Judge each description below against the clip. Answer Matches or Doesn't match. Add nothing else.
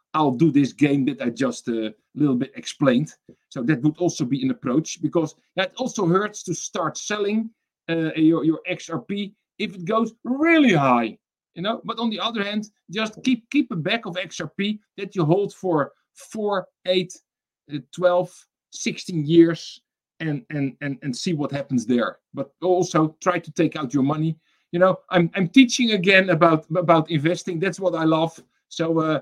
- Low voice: Doesn't match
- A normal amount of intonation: Matches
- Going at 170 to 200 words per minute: Matches